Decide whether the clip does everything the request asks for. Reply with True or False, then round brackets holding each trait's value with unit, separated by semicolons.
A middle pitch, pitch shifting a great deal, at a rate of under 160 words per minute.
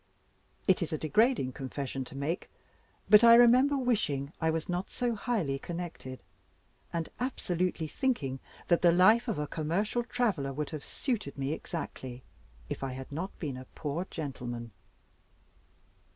True (165 Hz; 7.7 semitones; 150 wpm)